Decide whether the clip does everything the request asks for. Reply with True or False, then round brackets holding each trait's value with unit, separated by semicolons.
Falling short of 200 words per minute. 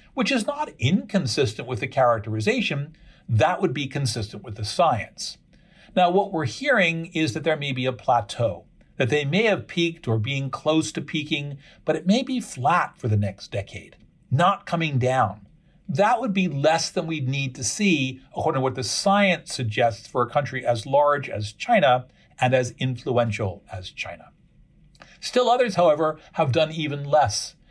True (175 wpm)